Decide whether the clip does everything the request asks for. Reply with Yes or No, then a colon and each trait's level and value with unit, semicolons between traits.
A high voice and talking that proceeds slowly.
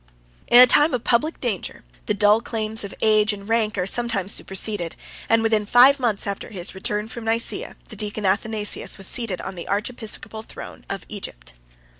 No: high, 215 Hz; average, 185 wpm